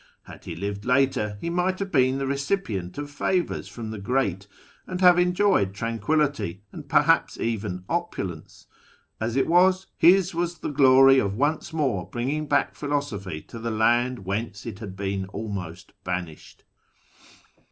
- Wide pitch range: Yes, wide, 7.3 semitones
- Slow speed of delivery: No, average, 150 wpm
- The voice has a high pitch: No, low, 125 Hz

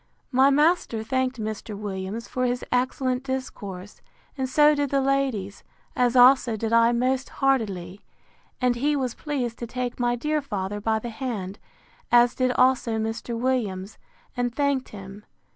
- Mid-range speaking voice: No, high, 245 Hz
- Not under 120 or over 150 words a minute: No, average, 160 wpm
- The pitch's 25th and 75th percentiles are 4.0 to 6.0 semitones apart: No, average, 3.3 semitones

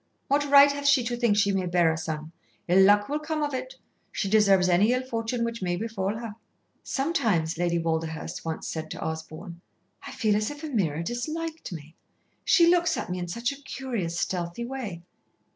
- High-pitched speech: Yes, high, 205 Hz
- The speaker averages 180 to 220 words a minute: Yes, average, 195 wpm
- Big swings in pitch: Yes, wide, 7.4 semitones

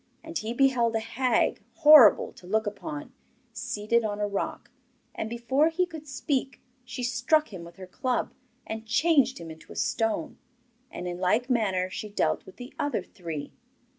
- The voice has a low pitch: No, high, 230 Hz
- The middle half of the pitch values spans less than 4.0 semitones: No, average, 4.7 semitones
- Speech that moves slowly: No, average, 170 wpm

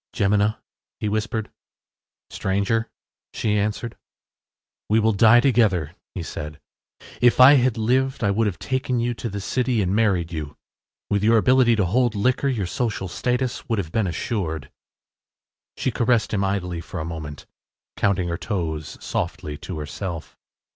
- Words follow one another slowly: No, average, 155 wpm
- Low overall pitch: Yes, low, 105 Hz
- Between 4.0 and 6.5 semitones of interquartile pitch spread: Yes, average, 4.8 semitones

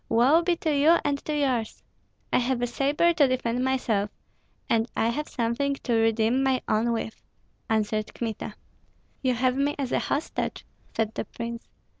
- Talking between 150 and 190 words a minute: Yes, average, 170 wpm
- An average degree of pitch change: Yes, average, 3.7 semitones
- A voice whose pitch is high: Yes, very high, 250 Hz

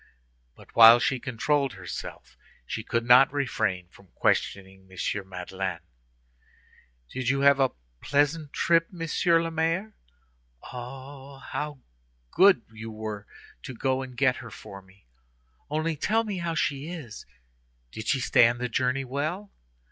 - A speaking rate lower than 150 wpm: Yes, average, 140 wpm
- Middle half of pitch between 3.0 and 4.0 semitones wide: No, average, 5.2 semitones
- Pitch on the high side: No, low, 130 Hz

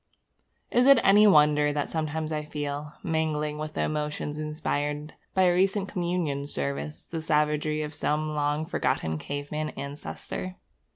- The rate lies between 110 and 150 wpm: Yes, average, 140 wpm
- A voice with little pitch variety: Yes, narrow, 1.4 semitones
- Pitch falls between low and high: Yes, medium, 150 Hz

